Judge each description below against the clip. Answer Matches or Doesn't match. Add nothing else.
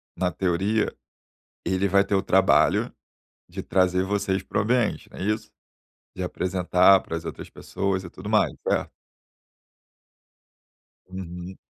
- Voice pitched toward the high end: Doesn't match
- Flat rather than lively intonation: Matches